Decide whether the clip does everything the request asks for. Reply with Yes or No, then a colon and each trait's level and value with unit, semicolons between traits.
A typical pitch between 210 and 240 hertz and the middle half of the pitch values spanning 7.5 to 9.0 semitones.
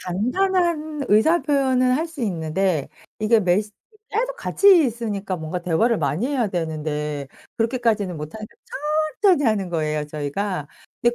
Yes: high, 215 Hz; wide, 8.4 semitones